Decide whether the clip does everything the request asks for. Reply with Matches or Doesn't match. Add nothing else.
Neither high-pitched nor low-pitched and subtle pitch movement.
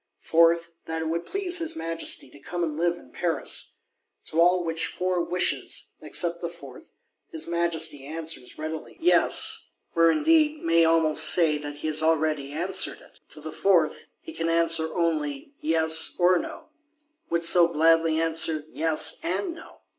Matches